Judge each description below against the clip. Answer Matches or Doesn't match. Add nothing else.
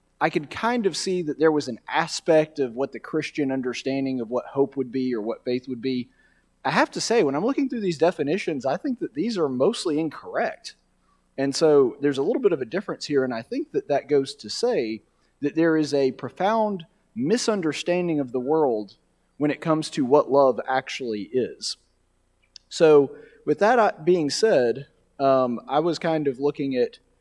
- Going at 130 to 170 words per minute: Doesn't match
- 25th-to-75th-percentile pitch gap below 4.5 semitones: Doesn't match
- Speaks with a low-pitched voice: Doesn't match